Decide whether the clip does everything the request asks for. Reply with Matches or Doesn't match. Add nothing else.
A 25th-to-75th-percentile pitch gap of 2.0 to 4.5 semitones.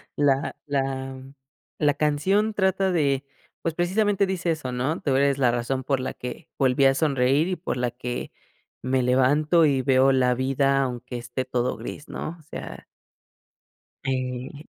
Matches